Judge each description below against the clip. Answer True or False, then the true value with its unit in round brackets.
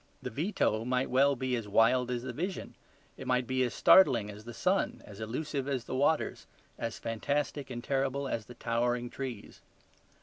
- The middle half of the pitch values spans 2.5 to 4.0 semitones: True (2.9 semitones)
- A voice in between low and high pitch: False (125 Hz)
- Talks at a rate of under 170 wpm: False (180 wpm)